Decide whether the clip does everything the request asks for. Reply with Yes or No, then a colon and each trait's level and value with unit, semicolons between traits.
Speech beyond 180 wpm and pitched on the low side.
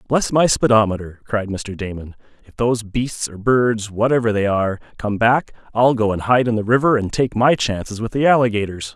Yes: average, 190 wpm; low, 115 Hz